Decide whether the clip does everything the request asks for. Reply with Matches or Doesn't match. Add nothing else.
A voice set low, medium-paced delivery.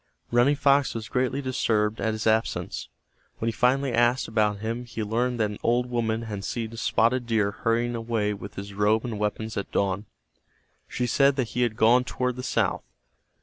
Matches